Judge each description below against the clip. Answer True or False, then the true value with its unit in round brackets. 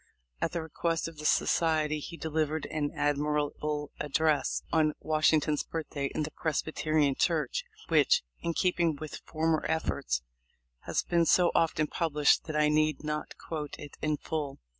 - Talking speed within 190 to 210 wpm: False (150 wpm)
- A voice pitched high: False (155 Hz)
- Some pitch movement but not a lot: False (1.3 semitones)